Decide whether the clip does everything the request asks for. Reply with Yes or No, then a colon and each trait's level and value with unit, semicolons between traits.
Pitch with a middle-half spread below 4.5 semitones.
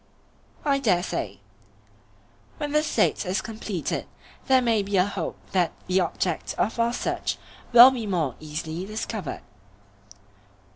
No: average, 4.8 semitones